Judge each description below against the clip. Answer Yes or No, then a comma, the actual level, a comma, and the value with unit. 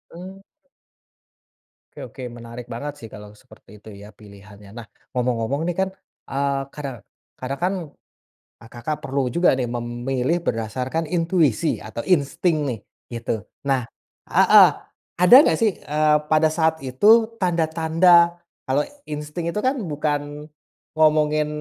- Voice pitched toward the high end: No, medium, 150 Hz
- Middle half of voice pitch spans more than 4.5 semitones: Yes, average, 5.3 semitones